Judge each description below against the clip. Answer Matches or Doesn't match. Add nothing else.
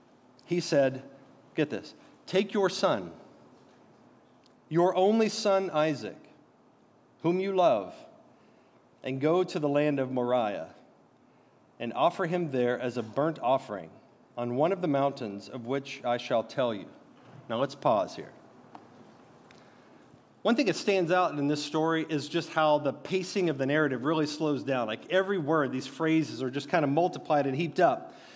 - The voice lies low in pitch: Doesn't match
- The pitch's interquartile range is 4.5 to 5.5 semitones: Matches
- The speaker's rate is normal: Matches